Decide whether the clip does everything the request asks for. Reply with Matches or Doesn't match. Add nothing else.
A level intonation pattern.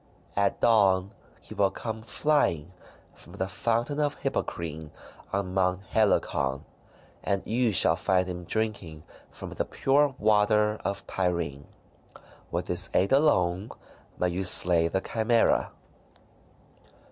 Doesn't match